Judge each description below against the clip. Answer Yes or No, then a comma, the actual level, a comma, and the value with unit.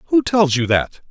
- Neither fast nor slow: No, fast, 215 wpm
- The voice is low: No, medium, 170 Hz